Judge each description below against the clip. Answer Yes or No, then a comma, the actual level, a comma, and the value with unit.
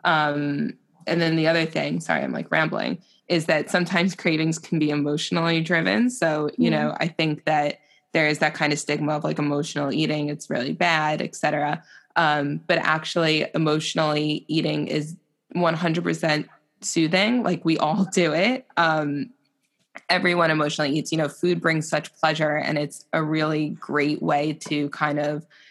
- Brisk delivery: No, average, 165 wpm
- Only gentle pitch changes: Yes, narrow, 1.9 semitones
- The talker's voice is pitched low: No, medium, 155 Hz